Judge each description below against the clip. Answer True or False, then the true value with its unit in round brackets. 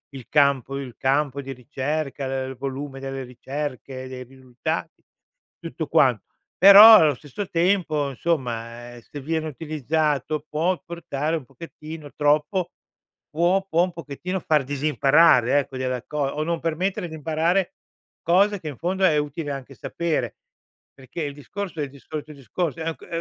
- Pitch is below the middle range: False (150 Hz)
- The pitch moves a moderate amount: True (3.5 semitones)